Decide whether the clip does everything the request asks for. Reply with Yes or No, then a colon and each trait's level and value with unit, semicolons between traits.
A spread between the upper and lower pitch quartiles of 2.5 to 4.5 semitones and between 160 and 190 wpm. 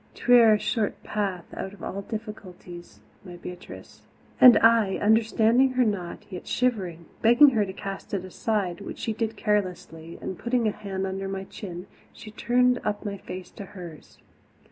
Yes: average, 3.4 semitones; average, 165 wpm